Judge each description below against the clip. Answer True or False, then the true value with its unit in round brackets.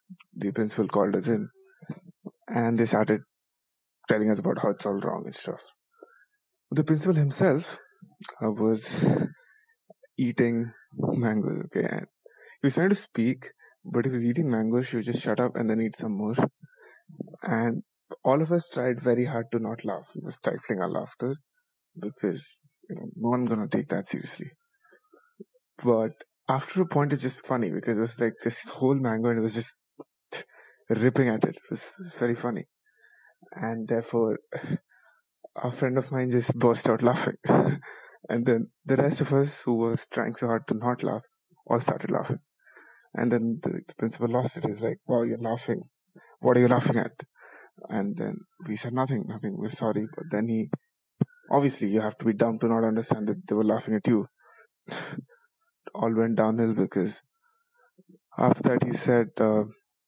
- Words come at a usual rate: True (175 wpm)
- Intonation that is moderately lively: False (7.2 semitones)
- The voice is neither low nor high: False (125 Hz)